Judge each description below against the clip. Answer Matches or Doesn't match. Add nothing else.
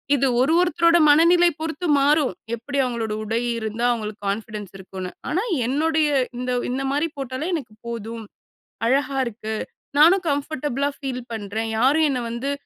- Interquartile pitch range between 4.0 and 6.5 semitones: Matches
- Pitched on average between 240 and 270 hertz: Matches